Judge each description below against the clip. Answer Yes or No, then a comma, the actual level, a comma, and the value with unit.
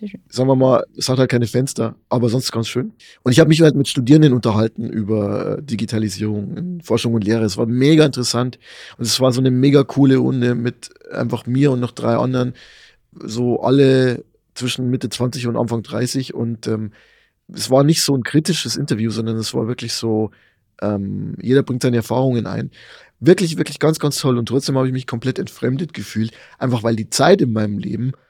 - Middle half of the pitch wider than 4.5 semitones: No, average, 2.9 semitones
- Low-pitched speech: Yes, low, 125 Hz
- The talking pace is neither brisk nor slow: No, fast, 195 wpm